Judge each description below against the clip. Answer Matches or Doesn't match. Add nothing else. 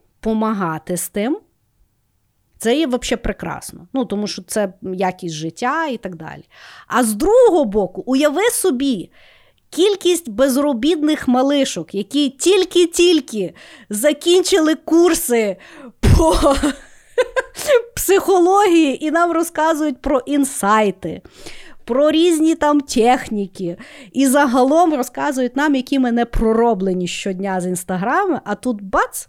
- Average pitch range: Doesn't match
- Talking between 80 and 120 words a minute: Matches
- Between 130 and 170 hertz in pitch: Doesn't match